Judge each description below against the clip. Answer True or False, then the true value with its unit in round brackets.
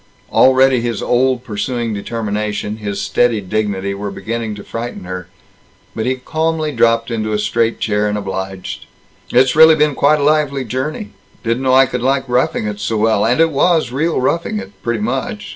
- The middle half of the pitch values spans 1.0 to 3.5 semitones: False (4.1 semitones)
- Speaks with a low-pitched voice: True (115 Hz)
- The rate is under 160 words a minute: False (180 wpm)